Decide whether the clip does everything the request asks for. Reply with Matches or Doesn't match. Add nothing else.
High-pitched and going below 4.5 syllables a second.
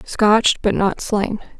Matches